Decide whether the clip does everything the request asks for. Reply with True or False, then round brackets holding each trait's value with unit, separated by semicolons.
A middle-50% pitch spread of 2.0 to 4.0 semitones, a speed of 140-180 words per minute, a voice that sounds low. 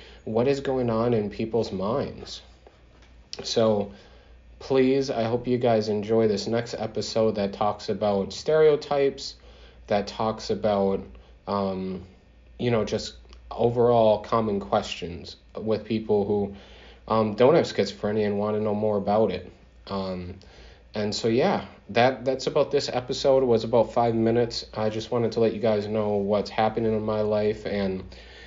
True (2.8 semitones; 155 wpm; 105 Hz)